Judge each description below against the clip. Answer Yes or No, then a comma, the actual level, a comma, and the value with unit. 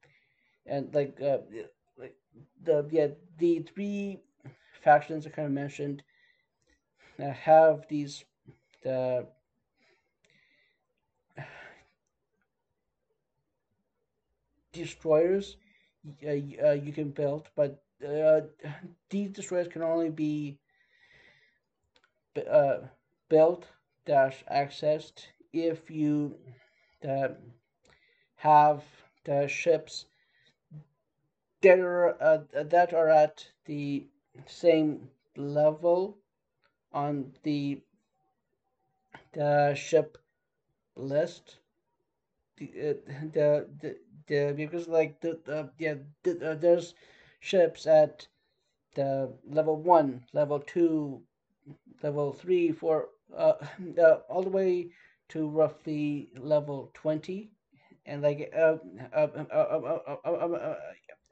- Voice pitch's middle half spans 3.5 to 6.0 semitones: No, average, 2.8 semitones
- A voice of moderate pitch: Yes, medium, 155 Hz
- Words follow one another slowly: Yes, slow, 95 wpm